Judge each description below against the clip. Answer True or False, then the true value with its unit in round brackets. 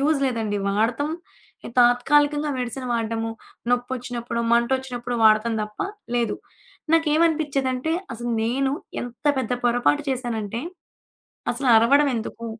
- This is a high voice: True (245 Hz)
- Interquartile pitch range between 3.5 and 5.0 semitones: False (2.9 semitones)